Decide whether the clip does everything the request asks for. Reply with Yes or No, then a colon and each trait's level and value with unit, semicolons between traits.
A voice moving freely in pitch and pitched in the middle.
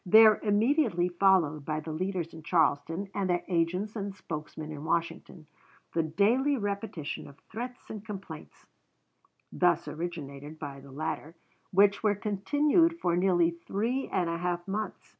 No: average, 4.2 semitones; medium, 180 Hz